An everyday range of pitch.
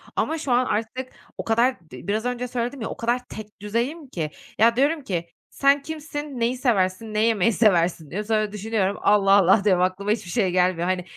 Yes: average, 4.4 semitones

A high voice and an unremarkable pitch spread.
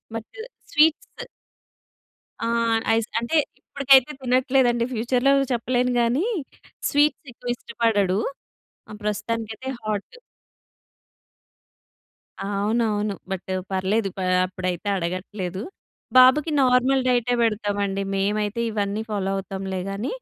Yes: high, 220 Hz; average, 4.1 semitones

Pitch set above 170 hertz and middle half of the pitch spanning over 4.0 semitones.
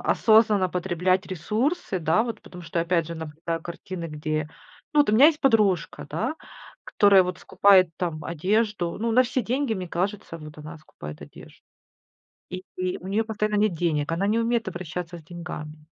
Yes: medium, 185 Hz; average, 4.4 semitones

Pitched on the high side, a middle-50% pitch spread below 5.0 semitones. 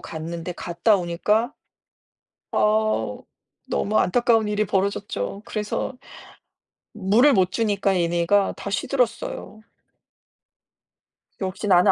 Yes: high, 200 Hz; average, 3.2 semitones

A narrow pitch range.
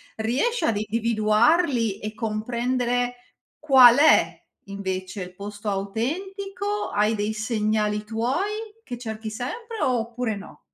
No: average, 3.6 semitones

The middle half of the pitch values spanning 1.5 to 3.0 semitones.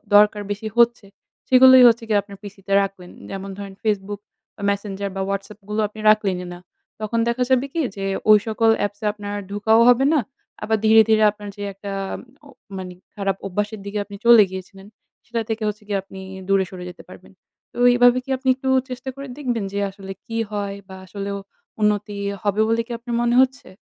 Yes: narrow, 2.6 semitones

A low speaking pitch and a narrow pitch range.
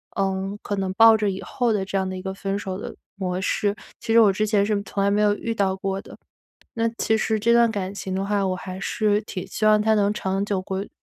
No: high, 200 Hz; narrow, 1.9 semitones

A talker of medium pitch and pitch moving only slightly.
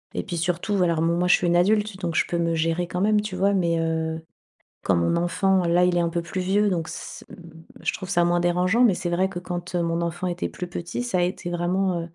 Yes: medium, 175 Hz; narrow, 1.7 semitones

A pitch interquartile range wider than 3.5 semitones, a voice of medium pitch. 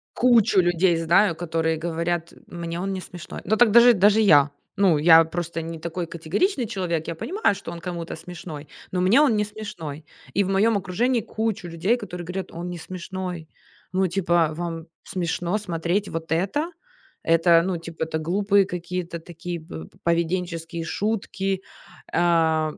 No: average, 2.9 semitones; medium, 175 Hz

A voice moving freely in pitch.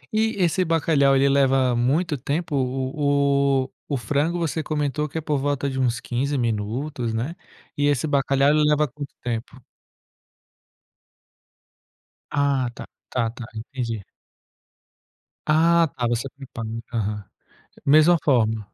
No: average, 3.6 semitones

